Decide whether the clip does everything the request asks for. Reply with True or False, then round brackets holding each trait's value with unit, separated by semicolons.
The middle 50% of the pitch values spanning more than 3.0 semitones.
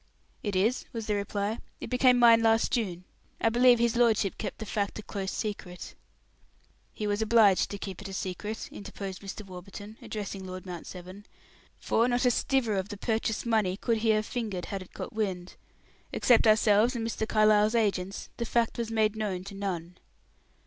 False (2.6 semitones)